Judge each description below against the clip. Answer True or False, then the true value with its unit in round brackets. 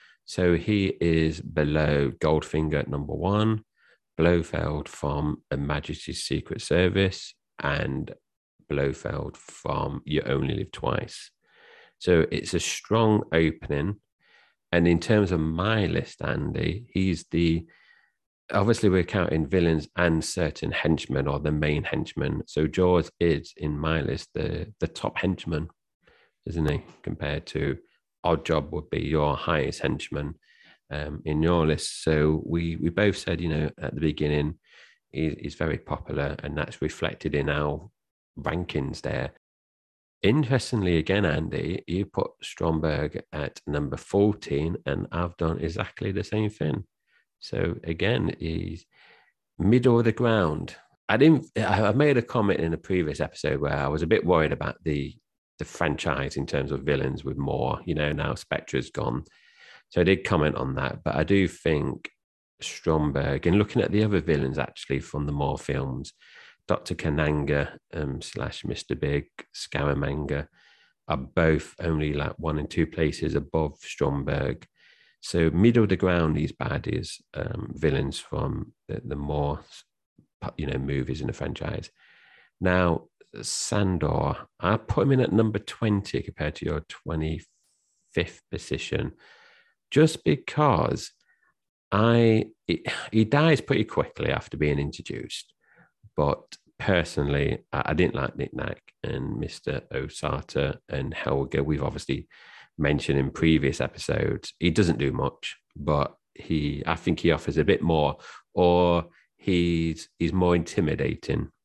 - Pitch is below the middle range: True (80 Hz)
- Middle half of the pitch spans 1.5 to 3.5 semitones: False (3.9 semitones)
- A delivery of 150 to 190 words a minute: False (140 wpm)